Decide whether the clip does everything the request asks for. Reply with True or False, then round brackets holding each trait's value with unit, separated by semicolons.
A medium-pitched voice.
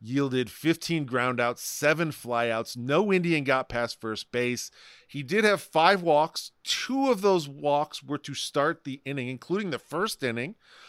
True (145 Hz)